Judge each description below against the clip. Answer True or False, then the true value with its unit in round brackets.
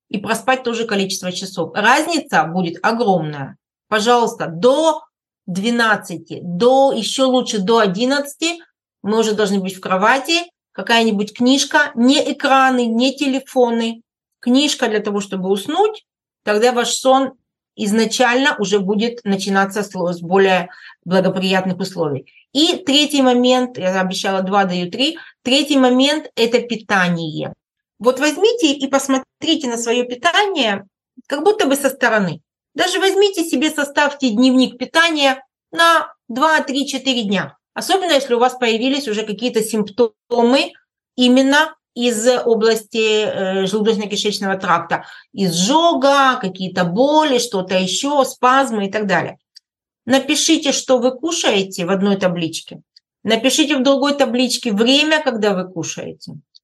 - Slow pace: True (120 wpm)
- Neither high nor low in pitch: False (245 Hz)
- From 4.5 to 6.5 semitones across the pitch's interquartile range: True (5.4 semitones)